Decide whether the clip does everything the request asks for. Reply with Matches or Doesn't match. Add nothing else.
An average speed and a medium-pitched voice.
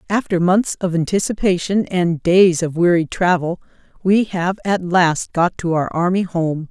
Matches